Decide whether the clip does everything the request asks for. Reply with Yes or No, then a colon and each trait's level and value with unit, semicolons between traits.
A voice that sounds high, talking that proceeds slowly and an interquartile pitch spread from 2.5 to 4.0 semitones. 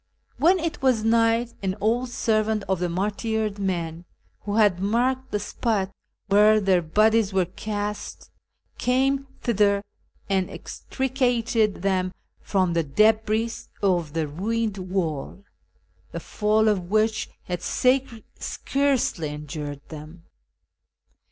Yes: high, 210 Hz; slow, 120 wpm; average, 3.7 semitones